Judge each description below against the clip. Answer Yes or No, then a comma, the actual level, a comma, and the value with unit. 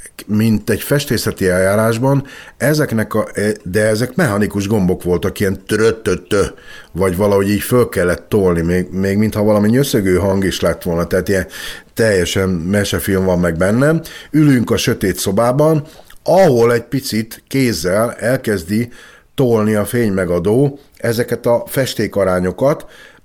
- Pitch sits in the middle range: No, low, 105 Hz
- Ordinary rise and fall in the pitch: Yes, average, 3.9 semitones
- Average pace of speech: Yes, average, 130 wpm